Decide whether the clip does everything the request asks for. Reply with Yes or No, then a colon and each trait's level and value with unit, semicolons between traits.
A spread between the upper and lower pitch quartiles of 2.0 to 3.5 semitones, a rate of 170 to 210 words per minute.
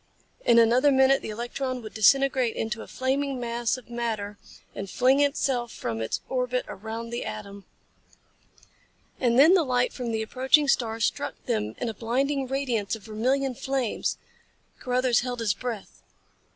No: average, 2.9 semitones; average, 155 wpm